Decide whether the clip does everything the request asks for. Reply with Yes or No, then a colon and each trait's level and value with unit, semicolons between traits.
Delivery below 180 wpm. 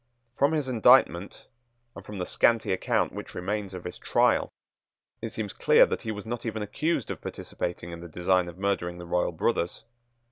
No: average, 185 wpm